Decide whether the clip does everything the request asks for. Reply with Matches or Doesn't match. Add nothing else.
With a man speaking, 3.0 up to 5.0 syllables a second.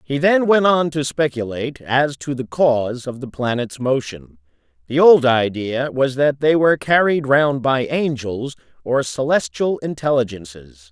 Matches